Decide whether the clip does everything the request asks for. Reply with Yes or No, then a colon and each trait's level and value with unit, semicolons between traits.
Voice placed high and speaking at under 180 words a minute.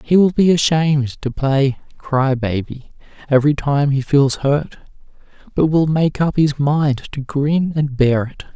No: medium, 145 Hz; average, 170 wpm